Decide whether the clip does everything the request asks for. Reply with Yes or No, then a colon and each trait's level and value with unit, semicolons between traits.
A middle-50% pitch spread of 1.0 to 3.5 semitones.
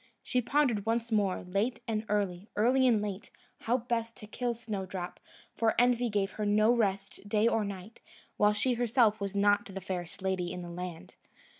Yes: average, 3.1 semitones